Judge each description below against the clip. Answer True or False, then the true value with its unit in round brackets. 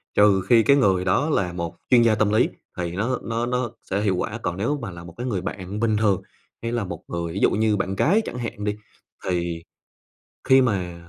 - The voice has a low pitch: True (105 Hz)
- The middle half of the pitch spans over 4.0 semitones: True (4.4 semitones)